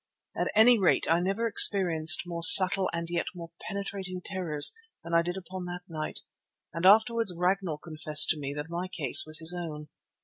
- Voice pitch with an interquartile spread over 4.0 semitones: No, average, 2.9 semitones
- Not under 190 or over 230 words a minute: No, average, 180 wpm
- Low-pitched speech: No, medium, 175 Hz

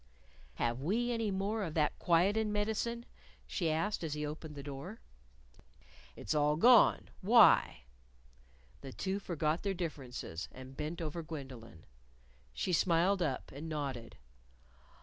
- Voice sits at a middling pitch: Yes, medium, 165 Hz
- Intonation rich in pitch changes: Yes, wide, 5.7 semitones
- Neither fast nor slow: No, slow, 130 wpm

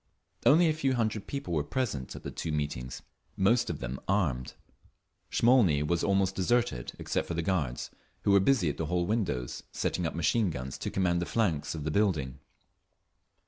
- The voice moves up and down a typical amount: No, wide, 6.7 semitones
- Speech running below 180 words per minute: No, average, 185 wpm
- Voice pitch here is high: No, very low, 85 Hz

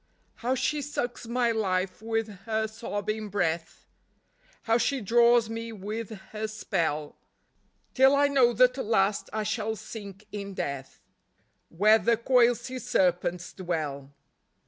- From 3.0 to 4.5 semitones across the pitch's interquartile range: Yes, average, 3.6 semitones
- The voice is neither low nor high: No, high, 220 Hz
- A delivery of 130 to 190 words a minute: Yes, slow, 135 wpm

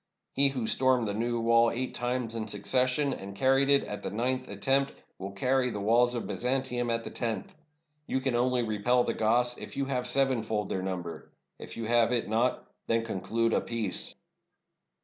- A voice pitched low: Yes, low, 120 Hz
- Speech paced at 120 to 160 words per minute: No, average, 190 wpm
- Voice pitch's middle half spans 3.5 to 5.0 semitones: No, narrow, 2.4 semitones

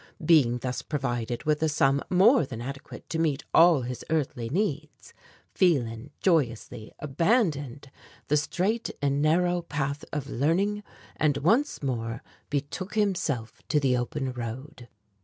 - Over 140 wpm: No, slow, 135 wpm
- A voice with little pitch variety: No, average, 4.7 semitones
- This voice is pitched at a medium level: Yes, medium, 145 Hz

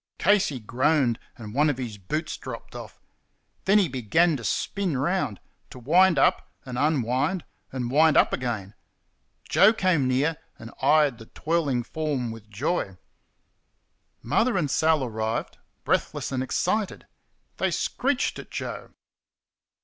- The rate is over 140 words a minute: No, slow, 135 wpm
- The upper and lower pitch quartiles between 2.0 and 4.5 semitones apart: No, wide, 5.5 semitones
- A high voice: No, medium, 140 Hz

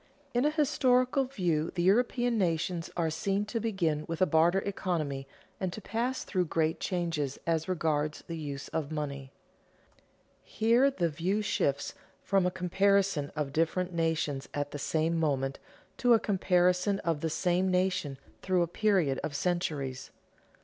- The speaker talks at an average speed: Yes, average, 155 wpm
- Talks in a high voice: No, medium, 175 Hz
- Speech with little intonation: No, average, 4.2 semitones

